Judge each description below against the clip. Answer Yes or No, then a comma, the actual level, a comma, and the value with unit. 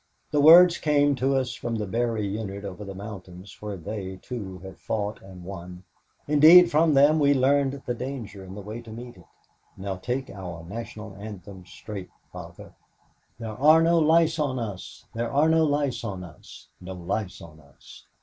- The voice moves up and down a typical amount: No, wide, 6.7 semitones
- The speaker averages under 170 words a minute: No, average, 180 wpm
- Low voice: Yes, low, 110 Hz